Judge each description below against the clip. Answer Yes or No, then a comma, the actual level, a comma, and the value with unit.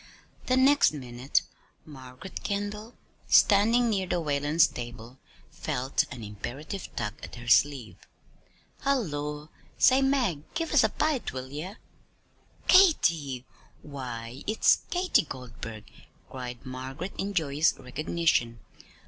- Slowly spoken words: Yes, slow, 115 wpm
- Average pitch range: No, wide, 8.2 semitones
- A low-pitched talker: No, medium, 150 Hz